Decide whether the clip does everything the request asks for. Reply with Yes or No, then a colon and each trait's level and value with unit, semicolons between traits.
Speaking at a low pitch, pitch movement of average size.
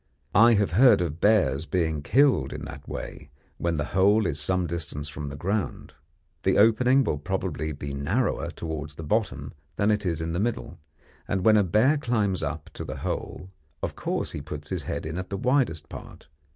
No: very low, 90 Hz; wide, 5.8 semitones